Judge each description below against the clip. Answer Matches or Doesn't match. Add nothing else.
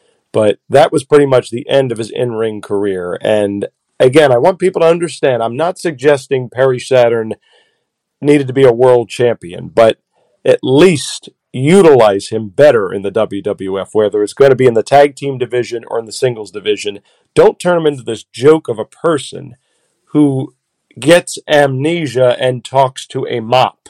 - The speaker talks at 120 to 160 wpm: Doesn't match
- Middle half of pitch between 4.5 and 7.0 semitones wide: Matches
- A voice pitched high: Doesn't match